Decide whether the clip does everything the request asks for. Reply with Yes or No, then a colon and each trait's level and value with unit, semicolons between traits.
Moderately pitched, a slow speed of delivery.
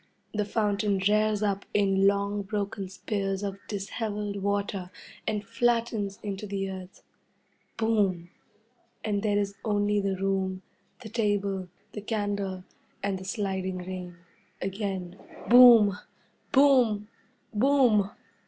No: high, 200 Hz; slow, 115 wpm